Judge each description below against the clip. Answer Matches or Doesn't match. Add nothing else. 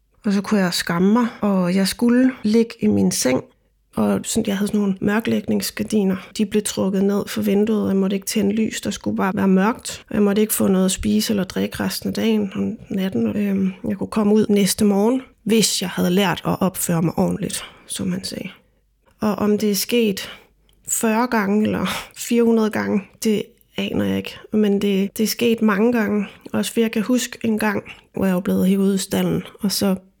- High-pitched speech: Matches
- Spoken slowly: Doesn't match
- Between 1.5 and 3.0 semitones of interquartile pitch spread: Matches